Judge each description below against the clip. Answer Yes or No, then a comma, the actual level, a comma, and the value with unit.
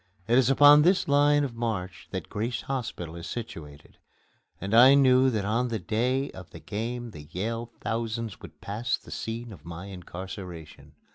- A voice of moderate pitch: No, low, 115 Hz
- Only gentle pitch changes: No, average, 5.1 semitones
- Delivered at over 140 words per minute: Yes, average, 170 wpm